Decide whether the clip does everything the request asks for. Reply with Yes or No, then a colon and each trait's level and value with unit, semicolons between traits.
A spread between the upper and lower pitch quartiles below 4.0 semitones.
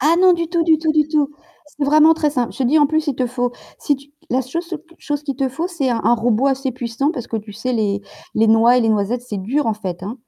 No: average, 4.8 semitones